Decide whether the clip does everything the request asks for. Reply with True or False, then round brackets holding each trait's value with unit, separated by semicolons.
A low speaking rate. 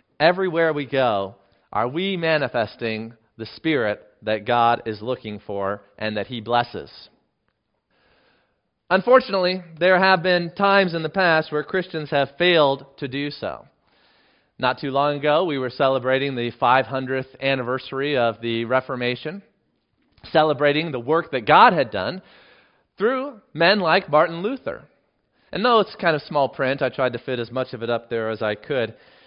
False (160 wpm)